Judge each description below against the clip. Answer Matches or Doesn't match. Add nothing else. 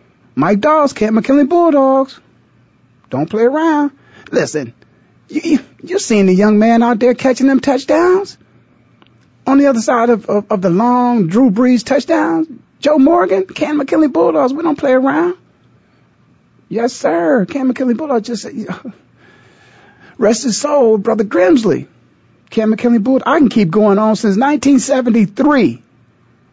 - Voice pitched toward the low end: Doesn't match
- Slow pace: Doesn't match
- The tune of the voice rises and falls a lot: Doesn't match